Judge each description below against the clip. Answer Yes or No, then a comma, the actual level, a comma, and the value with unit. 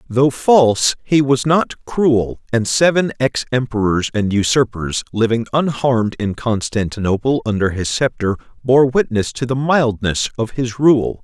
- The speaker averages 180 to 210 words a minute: No, average, 145 wpm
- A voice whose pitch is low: Yes, low, 120 Hz